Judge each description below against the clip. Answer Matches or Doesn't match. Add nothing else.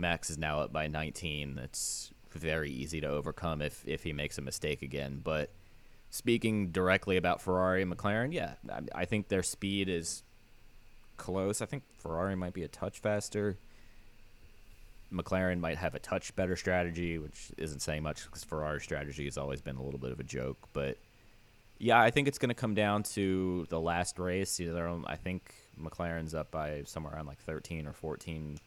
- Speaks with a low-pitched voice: Matches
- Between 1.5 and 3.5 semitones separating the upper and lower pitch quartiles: Doesn't match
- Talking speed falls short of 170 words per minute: Doesn't match